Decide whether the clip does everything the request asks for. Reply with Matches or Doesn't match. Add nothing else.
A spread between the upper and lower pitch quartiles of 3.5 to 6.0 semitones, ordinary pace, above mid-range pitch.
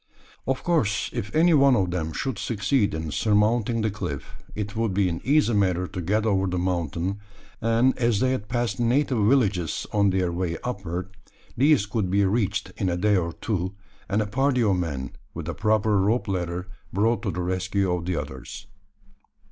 Doesn't match